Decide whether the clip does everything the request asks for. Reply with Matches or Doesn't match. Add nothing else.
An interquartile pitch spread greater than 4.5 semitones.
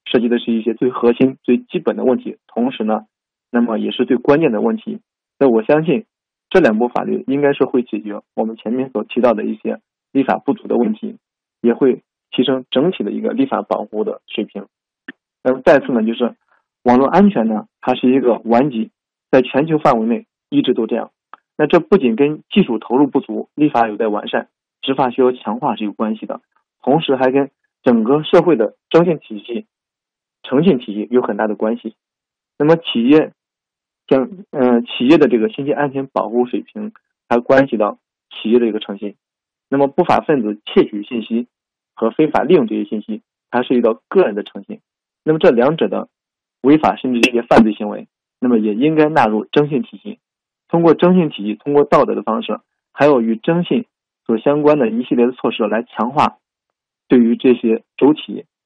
Matches